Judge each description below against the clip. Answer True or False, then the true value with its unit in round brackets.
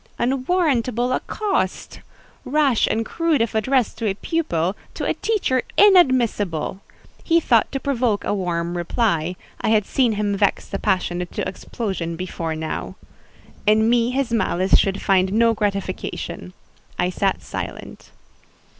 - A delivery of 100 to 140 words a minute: True (135 wpm)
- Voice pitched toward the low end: False (220 Hz)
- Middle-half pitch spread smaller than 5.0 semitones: False (5.5 semitones)